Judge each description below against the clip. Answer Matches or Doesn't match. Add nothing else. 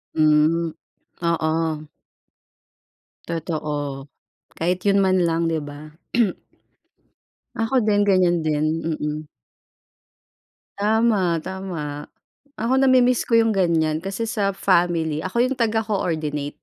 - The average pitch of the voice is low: Doesn't match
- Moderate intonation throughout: Matches